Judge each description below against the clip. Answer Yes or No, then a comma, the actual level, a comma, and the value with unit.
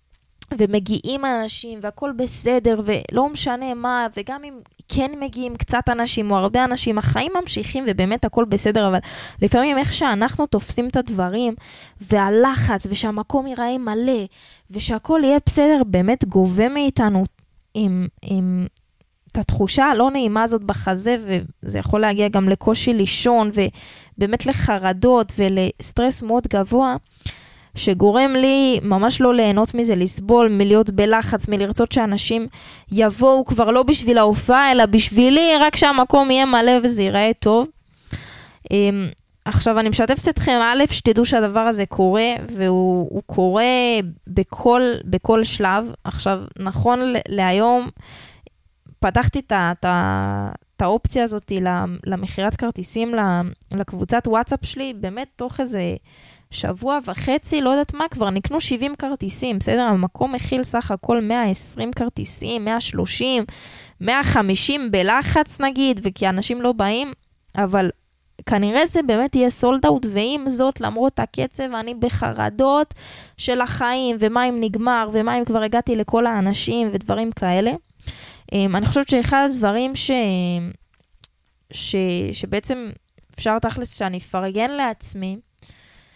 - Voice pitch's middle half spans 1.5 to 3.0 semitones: No, average, 4.0 semitones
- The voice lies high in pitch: Yes, high, 225 Hz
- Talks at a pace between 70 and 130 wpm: Yes, average, 120 wpm